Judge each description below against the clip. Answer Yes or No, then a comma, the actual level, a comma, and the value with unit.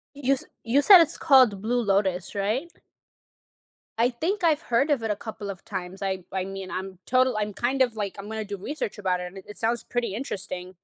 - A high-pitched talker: Yes, high, 215 Hz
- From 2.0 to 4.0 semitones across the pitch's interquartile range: No, average, 4.9 semitones